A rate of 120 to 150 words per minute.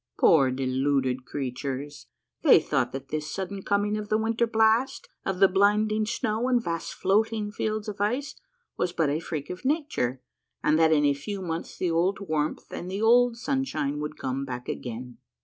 No: average, 180 wpm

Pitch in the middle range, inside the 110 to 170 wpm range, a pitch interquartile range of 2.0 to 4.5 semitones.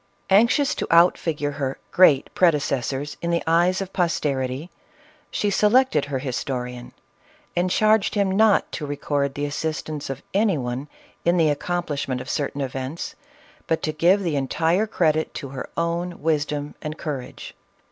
Yes: medium, 155 Hz; average, 165 wpm; average, 4.1 semitones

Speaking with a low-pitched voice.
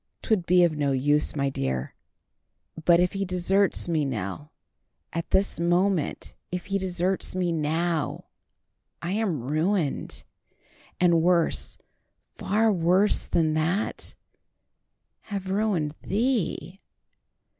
No: medium, 175 Hz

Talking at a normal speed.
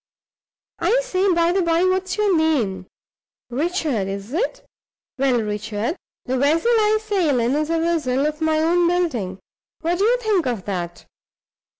Yes: average, 160 wpm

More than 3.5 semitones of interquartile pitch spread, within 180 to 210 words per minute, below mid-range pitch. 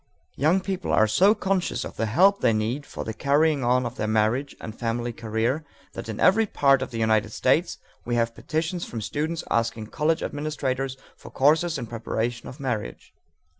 Yes: wide, 5.6 semitones; average, 185 wpm; low, 130 Hz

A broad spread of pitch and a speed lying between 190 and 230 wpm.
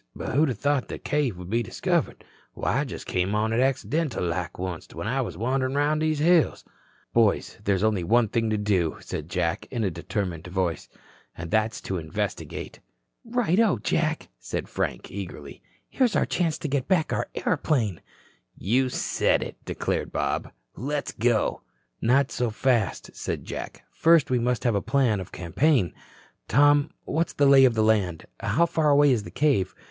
No: wide, 6.7 semitones; average, 175 wpm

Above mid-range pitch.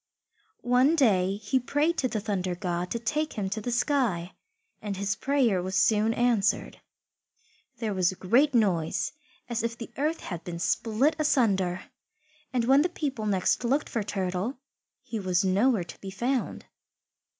Yes: high, 220 Hz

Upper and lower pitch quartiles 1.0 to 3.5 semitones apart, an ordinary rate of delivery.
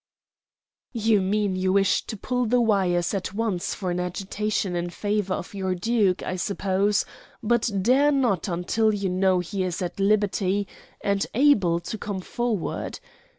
Yes: average, 2.8 semitones; average, 155 wpm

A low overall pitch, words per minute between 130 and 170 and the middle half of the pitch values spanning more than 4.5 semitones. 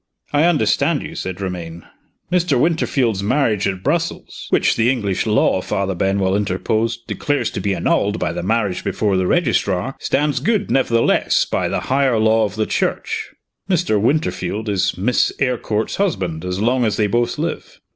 Yes: low, 110 Hz; average, 165 wpm; wide, 5.5 semitones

